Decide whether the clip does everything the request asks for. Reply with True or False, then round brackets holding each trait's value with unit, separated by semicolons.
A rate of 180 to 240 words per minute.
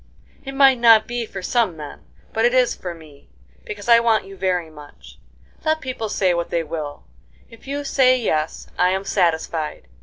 True (185 wpm)